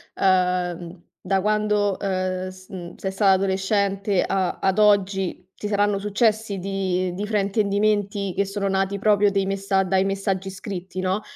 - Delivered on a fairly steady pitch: Yes, narrow, 1.4 semitones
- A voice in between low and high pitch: No, high, 195 Hz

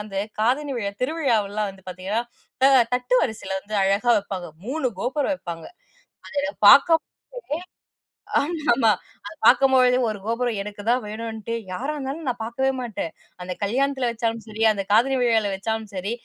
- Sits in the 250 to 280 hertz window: No, high, 230 Hz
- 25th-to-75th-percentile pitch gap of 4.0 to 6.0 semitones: Yes, average, 4.4 semitones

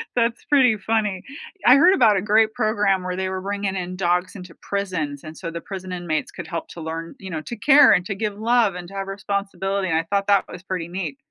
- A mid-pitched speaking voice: No, high, 195 Hz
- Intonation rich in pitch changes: No, average, 2.9 semitones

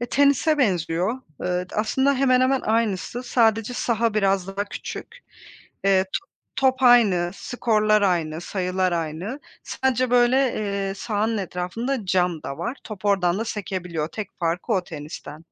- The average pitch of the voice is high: Yes, high, 205 Hz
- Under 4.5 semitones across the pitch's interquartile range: No, average, 5.2 semitones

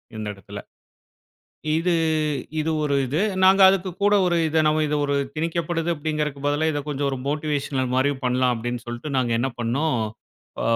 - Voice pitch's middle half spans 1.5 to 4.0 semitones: Yes, average, 3.7 semitones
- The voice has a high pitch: No, medium, 145 Hz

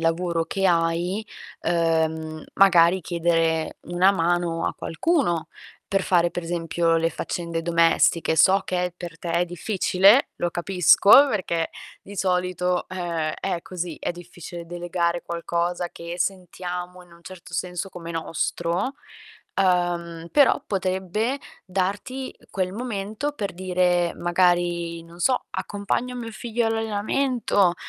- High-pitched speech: No, medium, 175 Hz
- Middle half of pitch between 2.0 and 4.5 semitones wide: Yes, narrow, 2.4 semitones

